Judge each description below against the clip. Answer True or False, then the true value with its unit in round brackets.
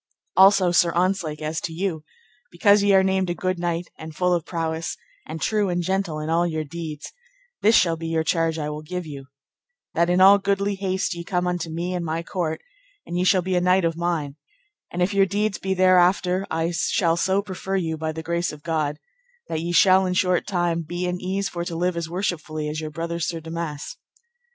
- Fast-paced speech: True (220 wpm)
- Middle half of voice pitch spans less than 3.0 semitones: True (2.4 semitones)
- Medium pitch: True (175 Hz)